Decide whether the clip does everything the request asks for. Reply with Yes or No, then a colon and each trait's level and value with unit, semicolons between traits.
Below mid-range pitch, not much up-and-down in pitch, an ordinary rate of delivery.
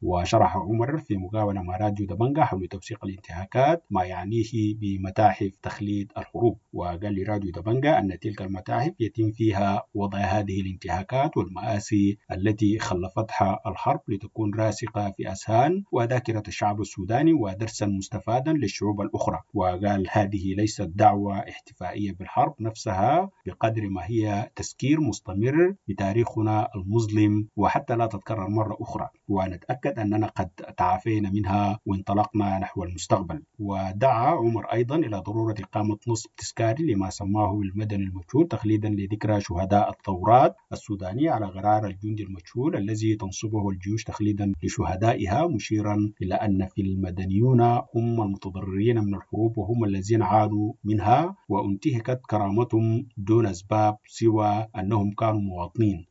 No: low, 105 Hz; narrow, 2.2 semitones; slow, 125 wpm